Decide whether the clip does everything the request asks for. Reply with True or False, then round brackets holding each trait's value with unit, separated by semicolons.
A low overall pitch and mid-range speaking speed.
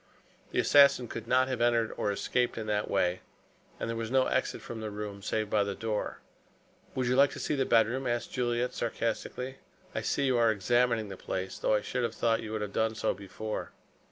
False (115 Hz; 215 wpm)